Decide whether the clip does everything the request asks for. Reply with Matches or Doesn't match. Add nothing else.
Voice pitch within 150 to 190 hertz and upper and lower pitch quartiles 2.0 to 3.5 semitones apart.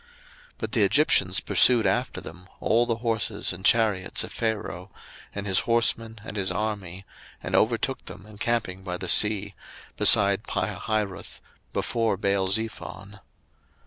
Doesn't match